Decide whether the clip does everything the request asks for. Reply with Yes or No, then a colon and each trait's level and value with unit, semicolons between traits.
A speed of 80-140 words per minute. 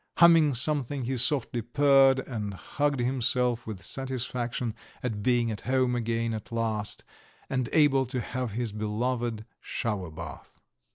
Yes: slow, 135 wpm